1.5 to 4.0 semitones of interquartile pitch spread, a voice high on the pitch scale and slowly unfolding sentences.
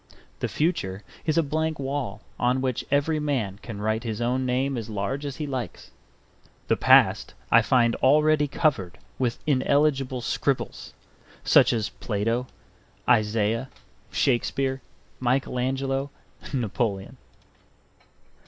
No: average, 3.4 semitones; low, 130 Hz; slow, 120 wpm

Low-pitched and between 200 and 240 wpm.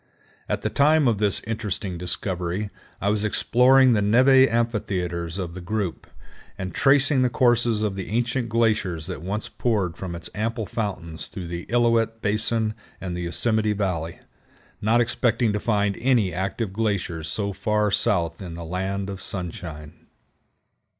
No: low, 105 Hz; average, 155 wpm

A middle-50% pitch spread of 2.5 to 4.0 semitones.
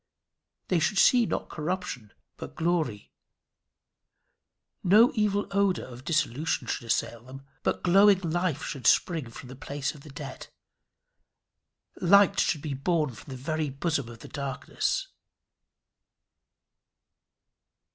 No: wide, 5.6 semitones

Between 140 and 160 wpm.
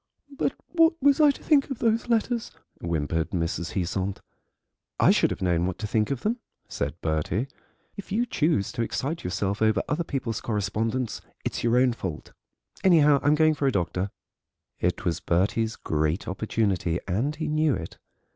No: average, 170 wpm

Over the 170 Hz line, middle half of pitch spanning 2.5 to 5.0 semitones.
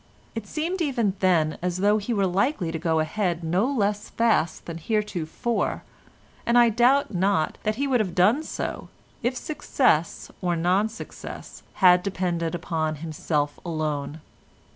No: medium, 185 Hz; wide, 5.6 semitones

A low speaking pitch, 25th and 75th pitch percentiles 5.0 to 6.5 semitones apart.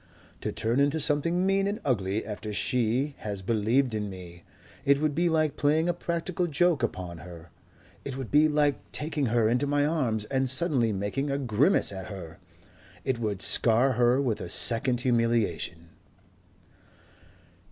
Yes: low, 125 Hz; wide, 5.6 semitones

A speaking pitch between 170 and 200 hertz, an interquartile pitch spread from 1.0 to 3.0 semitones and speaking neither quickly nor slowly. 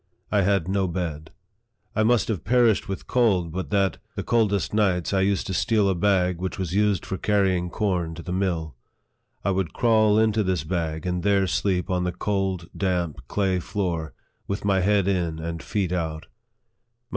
No: very low, 95 Hz; narrow, 2.6 semitones; average, 180 wpm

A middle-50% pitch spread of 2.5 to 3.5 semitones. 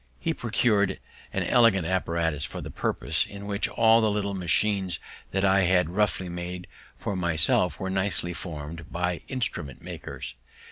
Yes: average, 2.8 semitones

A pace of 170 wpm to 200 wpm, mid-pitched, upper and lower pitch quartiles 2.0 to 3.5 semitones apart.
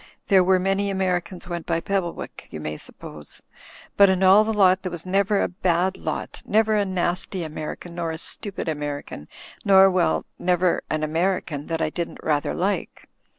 Yes: average, 180 wpm; medium, 180 Hz; average, 2.7 semitones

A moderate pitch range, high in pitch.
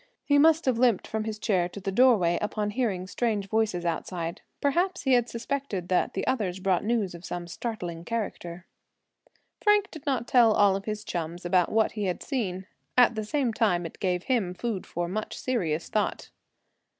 Yes: average, 5.0 semitones; high, 210 Hz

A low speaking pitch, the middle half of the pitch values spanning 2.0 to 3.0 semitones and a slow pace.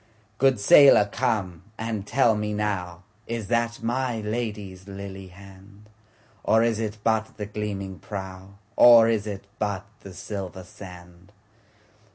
Yes: low, 105 Hz; narrow, 2.6 semitones; slow, 120 wpm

